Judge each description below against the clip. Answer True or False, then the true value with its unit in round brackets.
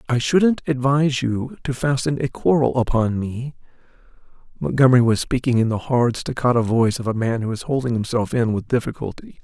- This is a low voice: True (125 Hz)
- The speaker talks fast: False (180 wpm)